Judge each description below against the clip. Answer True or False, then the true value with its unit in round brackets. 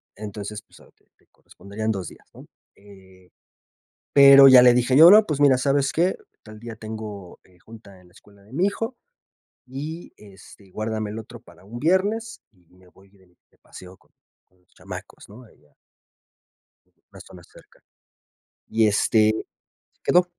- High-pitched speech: False (110 Hz)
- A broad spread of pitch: True (5.8 semitones)